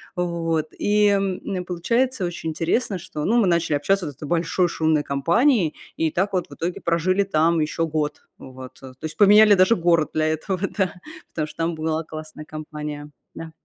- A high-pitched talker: No, medium, 165 Hz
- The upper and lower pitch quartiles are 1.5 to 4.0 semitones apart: Yes, average, 3.2 semitones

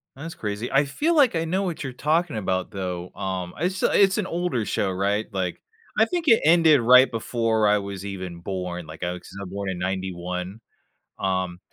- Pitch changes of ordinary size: No, wide, 9.0 semitones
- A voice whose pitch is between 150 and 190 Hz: No, low, 105 Hz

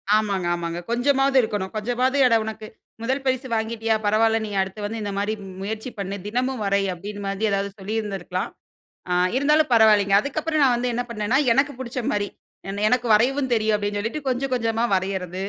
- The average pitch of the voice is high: Yes, high, 220 Hz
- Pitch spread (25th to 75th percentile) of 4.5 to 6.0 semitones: No, average, 3.7 semitones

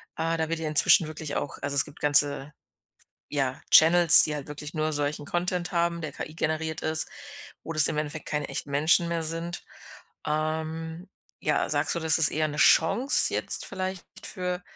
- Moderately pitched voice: Yes, medium, 160 Hz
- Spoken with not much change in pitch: Yes, narrow, 2.1 semitones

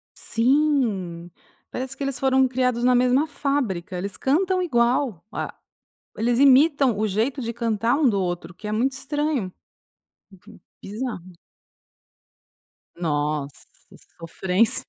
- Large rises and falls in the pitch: Yes, wide, 5.9 semitones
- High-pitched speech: Yes, high, 240 Hz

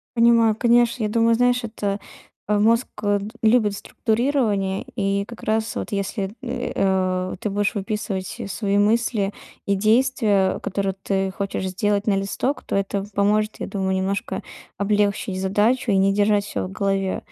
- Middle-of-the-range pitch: No, high, 205 Hz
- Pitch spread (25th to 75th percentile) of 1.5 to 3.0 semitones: Yes, narrow, 2.5 semitones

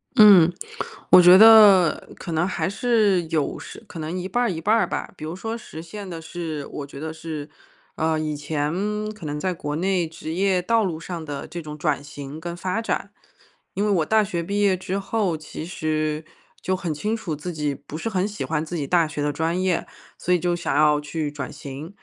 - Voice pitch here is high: No, medium, 170 Hz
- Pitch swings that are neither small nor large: Yes, average, 3.6 semitones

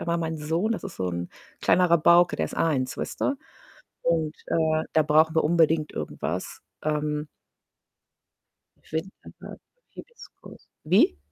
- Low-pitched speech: No, medium, 160 Hz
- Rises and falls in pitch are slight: Yes, narrow, 1.9 semitones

